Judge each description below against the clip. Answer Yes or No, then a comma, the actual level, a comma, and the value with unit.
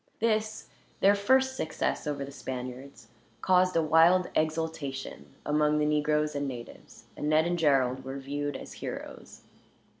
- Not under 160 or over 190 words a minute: No, average, 145 wpm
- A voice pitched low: No, medium, 150 Hz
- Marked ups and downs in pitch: No, average, 3.8 semitones